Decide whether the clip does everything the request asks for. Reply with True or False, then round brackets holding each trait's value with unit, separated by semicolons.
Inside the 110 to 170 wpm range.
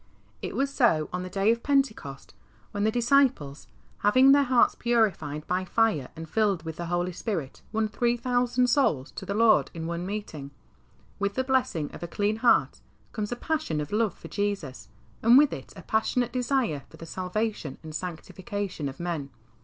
False (185 wpm)